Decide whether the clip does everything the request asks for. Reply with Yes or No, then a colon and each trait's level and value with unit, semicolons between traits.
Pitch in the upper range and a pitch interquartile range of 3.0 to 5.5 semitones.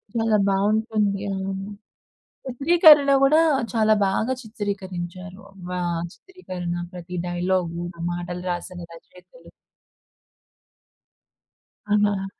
Yes: high, 195 Hz; average, 3.7 semitones